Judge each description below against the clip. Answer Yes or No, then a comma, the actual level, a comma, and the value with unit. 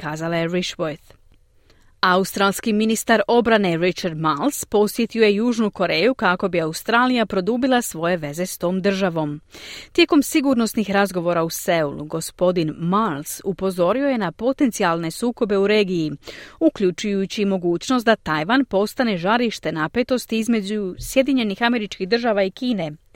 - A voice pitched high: Yes, high, 200 Hz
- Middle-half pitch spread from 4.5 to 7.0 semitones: Yes, average, 5.1 semitones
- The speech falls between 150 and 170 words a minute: No, average, 125 wpm